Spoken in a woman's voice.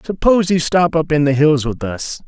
No: male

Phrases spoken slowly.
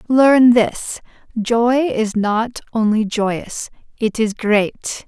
Yes: slow, 120 wpm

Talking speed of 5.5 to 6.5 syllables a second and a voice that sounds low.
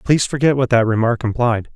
Yes: 6.1 syllables/s; low, 120 Hz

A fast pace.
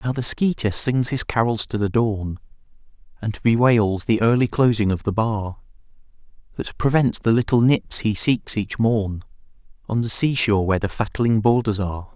No: average, 175 wpm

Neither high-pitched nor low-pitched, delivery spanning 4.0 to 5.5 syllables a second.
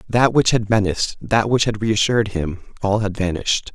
No: low, 105 Hz; 5.4 syllables/s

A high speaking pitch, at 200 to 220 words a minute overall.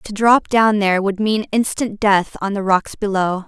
Yes: high, 205 Hz; fast, 205 wpm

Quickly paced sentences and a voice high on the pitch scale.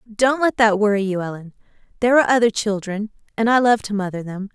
Yes: fast, 210 wpm; high, 215 Hz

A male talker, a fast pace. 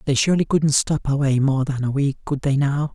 Yes: male; fast, 245 wpm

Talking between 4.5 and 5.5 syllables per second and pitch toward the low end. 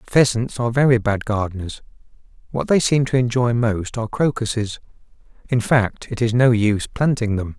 Yes: 5.3 syllables/s; low, 115 Hz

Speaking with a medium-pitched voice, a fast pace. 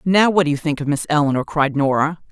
Yes: medium, 155 Hz; fast, 260 wpm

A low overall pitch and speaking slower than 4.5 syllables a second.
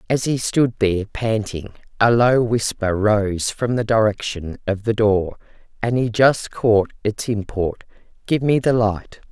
Yes: low, 110 Hz; 4.1 syllables/s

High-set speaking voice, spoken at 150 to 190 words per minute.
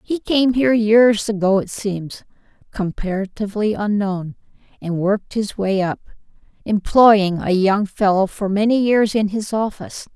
No: high, 205 Hz; average, 140 wpm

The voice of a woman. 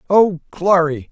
No: male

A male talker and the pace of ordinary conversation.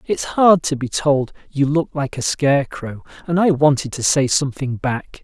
Yes: male; average, 195 wpm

